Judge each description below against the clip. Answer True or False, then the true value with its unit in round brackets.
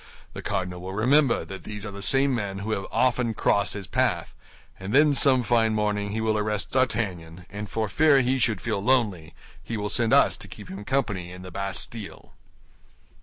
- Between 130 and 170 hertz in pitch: False (105 Hz)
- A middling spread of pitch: True (3.9 semitones)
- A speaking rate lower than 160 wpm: False (195 wpm)